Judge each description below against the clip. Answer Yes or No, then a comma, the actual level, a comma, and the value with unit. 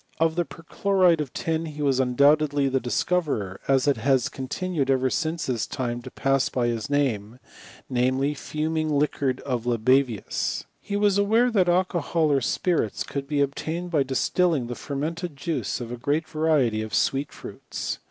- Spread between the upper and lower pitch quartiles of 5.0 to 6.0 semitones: No, average, 4.1 semitones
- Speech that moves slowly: No, average, 175 wpm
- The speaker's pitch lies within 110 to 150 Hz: Yes, medium, 140 Hz